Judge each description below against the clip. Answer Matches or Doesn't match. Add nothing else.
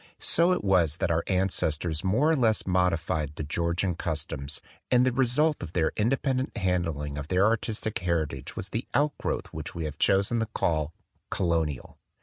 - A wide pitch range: Matches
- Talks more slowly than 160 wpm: Doesn't match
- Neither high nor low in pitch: Doesn't match